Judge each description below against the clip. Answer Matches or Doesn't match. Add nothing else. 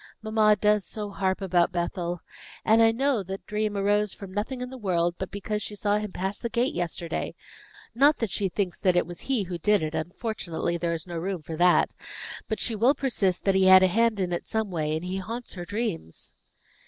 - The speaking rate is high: Matches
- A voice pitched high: Matches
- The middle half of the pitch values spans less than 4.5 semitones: Matches